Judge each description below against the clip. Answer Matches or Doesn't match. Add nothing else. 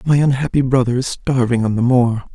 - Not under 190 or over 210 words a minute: Matches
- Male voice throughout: Matches